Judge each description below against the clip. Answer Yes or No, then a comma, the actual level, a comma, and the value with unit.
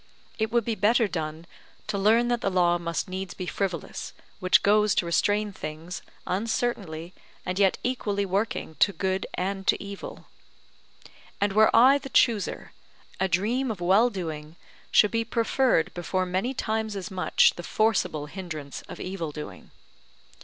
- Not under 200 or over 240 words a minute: No, average, 155 wpm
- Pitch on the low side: No, high, 195 Hz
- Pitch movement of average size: Yes, average, 3.8 semitones